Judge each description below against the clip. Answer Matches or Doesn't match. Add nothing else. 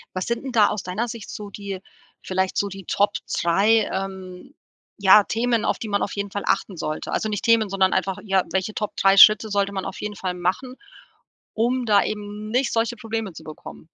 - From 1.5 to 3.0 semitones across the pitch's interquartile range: Matches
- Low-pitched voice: Doesn't match